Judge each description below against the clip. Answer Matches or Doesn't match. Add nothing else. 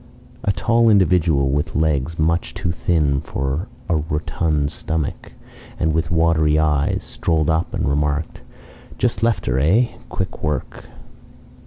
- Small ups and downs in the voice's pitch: Matches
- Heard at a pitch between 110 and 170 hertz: Doesn't match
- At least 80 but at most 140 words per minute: Matches